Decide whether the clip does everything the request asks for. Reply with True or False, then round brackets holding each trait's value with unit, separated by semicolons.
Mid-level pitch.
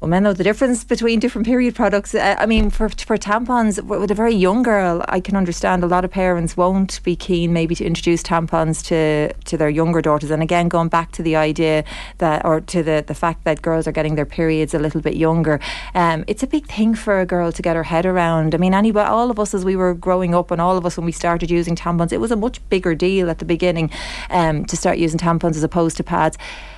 True (175 Hz)